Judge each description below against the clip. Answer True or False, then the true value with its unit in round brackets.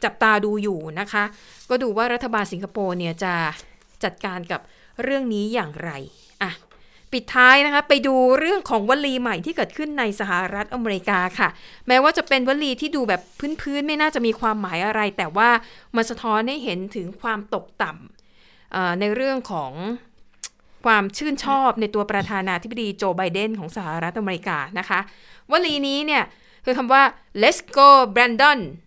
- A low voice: False (225 Hz)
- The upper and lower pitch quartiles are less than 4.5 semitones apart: False (5.1 semitones)